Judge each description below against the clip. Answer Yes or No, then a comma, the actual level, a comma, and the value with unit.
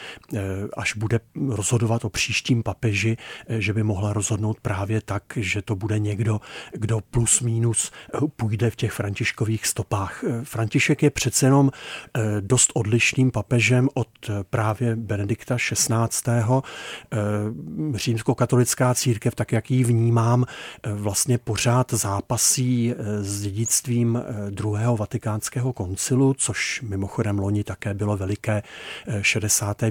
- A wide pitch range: No, average, 2.7 semitones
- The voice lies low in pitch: Yes, low, 115 Hz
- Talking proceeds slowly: Yes, slow, 110 wpm